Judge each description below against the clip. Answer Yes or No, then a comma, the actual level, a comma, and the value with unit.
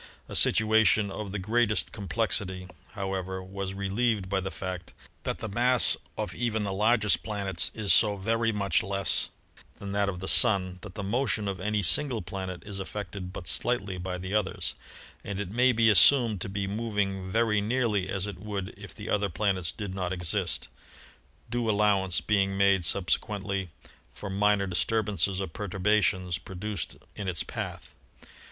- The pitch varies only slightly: Yes, narrow, 2.1 semitones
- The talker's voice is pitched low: Yes, low, 100 Hz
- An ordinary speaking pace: Yes, average, 165 wpm